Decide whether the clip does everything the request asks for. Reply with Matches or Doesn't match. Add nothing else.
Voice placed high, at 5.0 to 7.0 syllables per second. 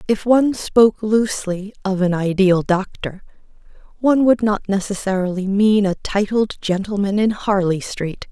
Doesn't match